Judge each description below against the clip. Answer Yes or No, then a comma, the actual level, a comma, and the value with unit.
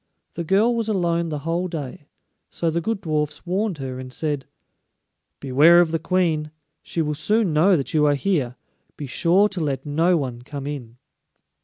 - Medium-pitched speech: Yes, medium, 160 Hz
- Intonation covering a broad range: No, average, 3.8 semitones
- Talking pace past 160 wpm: Yes, average, 180 wpm